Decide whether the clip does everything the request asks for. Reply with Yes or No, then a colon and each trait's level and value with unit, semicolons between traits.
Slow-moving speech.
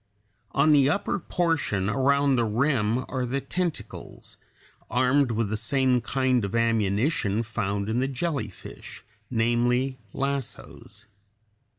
Yes: slow, 130 wpm